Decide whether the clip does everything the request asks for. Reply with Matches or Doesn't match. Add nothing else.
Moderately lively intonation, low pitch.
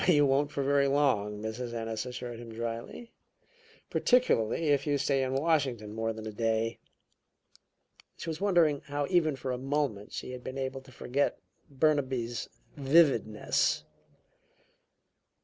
Matches